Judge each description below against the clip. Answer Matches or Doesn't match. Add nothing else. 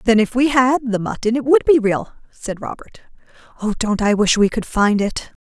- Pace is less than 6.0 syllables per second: Matches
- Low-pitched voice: Doesn't match